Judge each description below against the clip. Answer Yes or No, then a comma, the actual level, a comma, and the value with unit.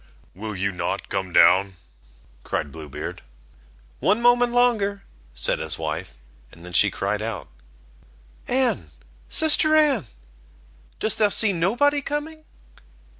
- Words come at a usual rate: No, slow, 125 wpm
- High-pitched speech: Yes, high, 200 Hz